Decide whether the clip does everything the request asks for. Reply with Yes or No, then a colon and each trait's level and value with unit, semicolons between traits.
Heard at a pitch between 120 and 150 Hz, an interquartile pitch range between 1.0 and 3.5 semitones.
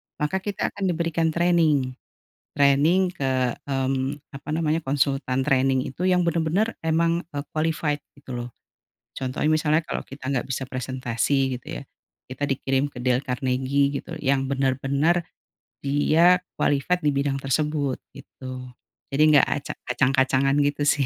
Yes: medium, 140 Hz; average, 3.1 semitones